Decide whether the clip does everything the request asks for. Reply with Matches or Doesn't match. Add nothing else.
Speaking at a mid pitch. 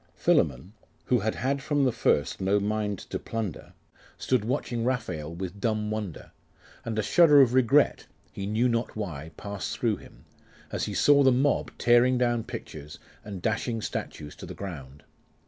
Doesn't match